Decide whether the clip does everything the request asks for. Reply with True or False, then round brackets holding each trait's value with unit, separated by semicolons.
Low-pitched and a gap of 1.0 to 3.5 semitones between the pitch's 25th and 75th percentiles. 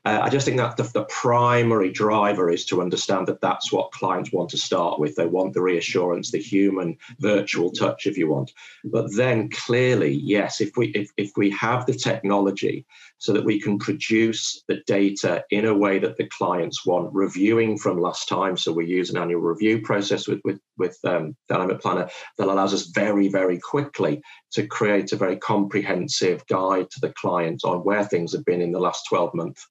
True (100 Hz; 2.8 semitones)